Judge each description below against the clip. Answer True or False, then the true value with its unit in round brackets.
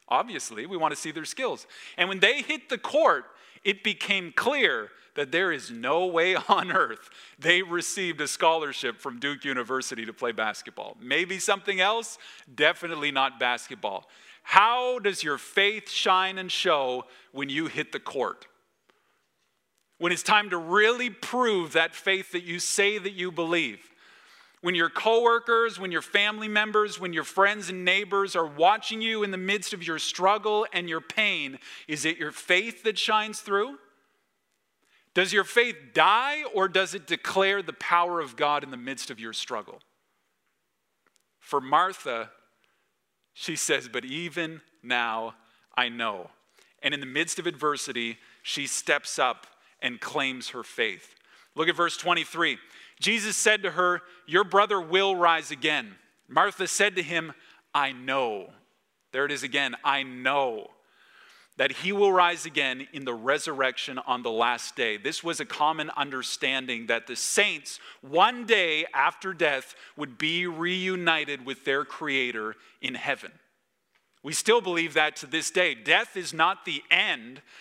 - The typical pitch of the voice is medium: True (175 Hz)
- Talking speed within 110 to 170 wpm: True (160 wpm)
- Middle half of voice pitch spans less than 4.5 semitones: False (5.1 semitones)